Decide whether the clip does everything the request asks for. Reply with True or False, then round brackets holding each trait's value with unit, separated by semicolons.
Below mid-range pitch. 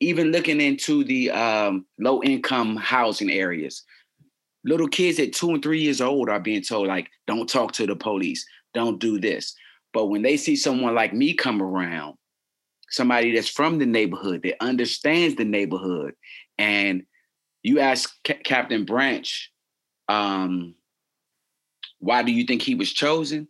True (125 Hz)